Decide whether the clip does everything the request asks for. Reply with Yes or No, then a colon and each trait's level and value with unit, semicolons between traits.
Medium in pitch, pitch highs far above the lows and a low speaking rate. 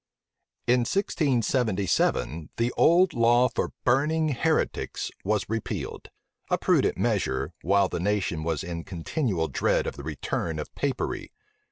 No: low, 115 Hz; wide, 7.9 semitones; slow, 130 wpm